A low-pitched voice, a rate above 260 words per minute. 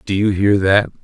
No: low, 100 Hz; fast, 230 wpm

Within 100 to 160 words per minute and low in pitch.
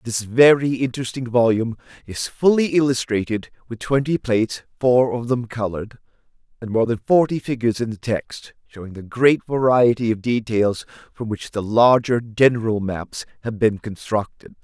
Yes: average, 150 wpm; low, 120 Hz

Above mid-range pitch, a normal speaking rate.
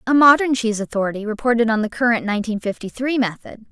Yes: high, 230 Hz; average, 195 wpm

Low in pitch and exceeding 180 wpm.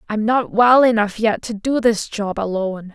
No: high, 220 Hz; fast, 205 wpm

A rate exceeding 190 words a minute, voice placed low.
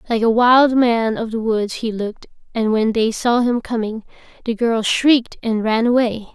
No: average, 200 wpm; high, 230 Hz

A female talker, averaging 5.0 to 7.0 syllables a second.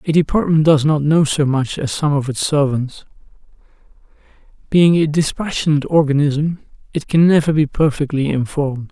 No: male; 5.3 syllables/s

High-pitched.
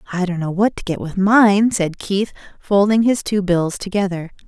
Yes: high, 195 Hz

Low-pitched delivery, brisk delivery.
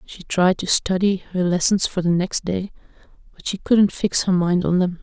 No: medium, 185 Hz; fast, 215 wpm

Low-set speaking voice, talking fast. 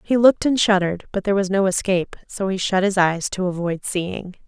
No: high, 190 Hz; fast, 230 wpm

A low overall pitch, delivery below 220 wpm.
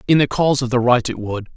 No: low, 125 Hz; fast, 310 wpm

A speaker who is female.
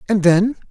No: male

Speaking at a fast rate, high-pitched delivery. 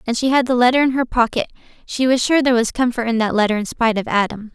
Yes: fast, 275 wpm; high, 240 Hz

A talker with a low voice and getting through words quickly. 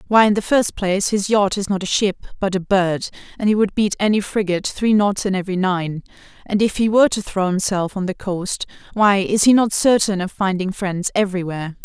No: high, 195 Hz; fast, 225 wpm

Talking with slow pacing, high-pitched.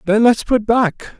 No: average, 200 wpm; high, 220 Hz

